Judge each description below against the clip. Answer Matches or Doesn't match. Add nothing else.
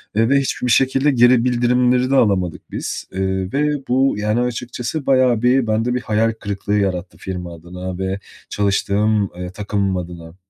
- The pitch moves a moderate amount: Matches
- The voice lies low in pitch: Matches